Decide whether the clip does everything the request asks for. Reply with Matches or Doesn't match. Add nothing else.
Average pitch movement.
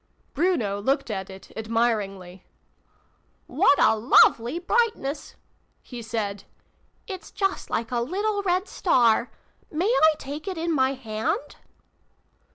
Doesn't match